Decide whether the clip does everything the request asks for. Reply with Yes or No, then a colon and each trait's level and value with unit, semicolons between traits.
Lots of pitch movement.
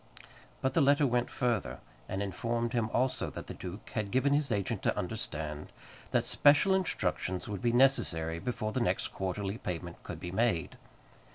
Yes: wide, 6.0 semitones